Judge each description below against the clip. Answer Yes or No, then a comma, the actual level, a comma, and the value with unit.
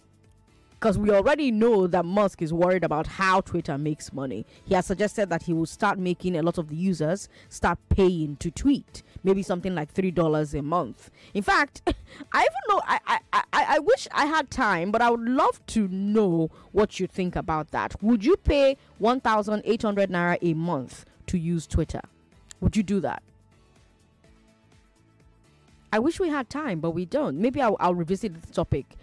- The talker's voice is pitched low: No, medium, 185 Hz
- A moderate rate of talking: Yes, average, 180 wpm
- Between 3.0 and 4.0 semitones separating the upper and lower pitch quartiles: No, average, 5.1 semitones